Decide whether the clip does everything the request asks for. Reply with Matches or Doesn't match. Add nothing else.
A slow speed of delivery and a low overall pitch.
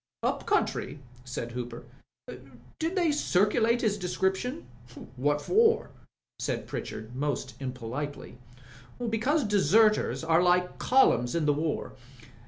Doesn't match